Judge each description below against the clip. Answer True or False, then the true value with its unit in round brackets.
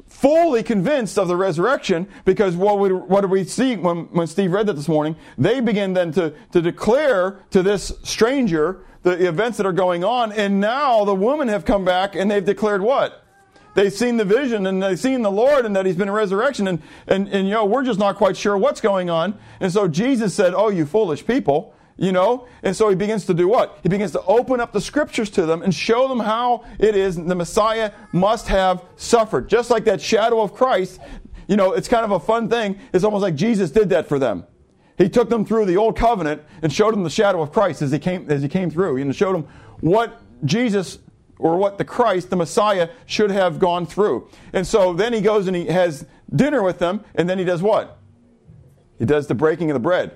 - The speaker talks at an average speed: False (230 wpm)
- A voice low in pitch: False (195 Hz)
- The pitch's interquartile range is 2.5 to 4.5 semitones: True (3.5 semitones)